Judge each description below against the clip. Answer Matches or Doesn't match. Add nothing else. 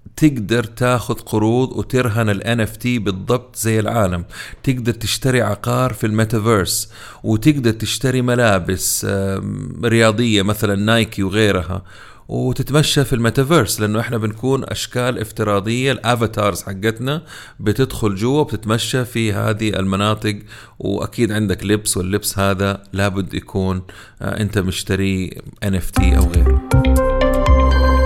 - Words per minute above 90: Matches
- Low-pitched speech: Matches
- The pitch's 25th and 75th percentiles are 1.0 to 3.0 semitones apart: Doesn't match